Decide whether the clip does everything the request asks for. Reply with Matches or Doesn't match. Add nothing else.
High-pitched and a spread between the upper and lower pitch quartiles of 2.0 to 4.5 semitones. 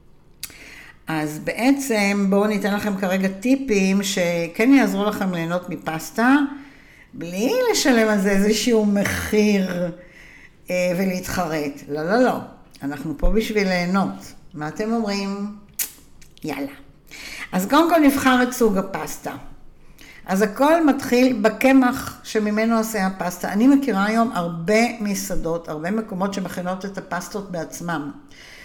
Matches